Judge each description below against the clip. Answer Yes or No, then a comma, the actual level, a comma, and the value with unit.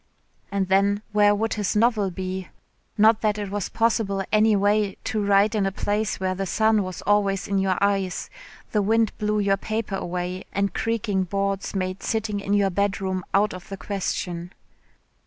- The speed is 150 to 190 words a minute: Yes, average, 175 wpm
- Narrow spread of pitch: Yes, narrow, 1.7 semitones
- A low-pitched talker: No, high, 200 Hz